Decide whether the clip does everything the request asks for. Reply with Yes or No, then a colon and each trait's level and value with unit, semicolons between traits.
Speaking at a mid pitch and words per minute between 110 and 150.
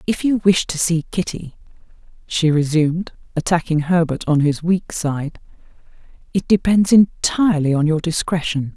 Yes: medium, 165 Hz; slow, 135 wpm